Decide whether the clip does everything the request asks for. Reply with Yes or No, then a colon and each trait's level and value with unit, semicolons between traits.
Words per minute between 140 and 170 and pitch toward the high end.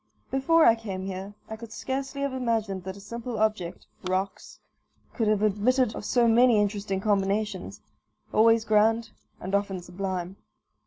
Yes: average, 150 wpm; high, 215 Hz